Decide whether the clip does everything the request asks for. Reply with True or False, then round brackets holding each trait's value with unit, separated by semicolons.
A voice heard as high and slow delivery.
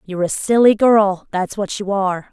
False (200 Hz; 205 wpm)